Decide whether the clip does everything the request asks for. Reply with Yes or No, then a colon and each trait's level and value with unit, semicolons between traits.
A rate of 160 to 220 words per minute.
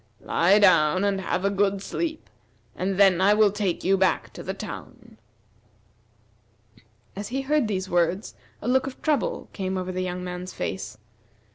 Yes: average, 165 wpm